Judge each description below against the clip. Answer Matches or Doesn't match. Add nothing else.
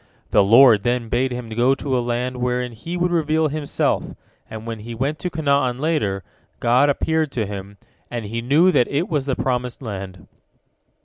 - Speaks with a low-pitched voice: Matches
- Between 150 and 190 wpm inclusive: Matches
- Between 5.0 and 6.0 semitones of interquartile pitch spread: Doesn't match